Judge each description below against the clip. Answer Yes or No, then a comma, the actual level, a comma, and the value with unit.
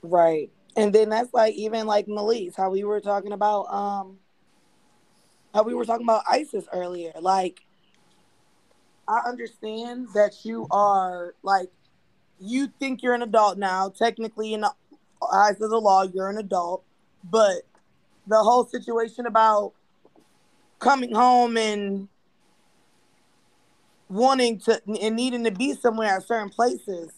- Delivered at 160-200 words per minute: No, slow, 135 wpm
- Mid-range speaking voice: No, high, 215 Hz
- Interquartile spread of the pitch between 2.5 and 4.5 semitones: Yes, average, 3.1 semitones